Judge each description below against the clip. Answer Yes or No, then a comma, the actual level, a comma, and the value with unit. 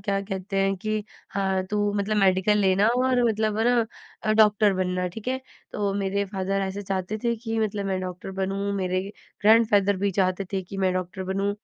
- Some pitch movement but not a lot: No, narrow, 2.1 semitones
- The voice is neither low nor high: No, high, 200 Hz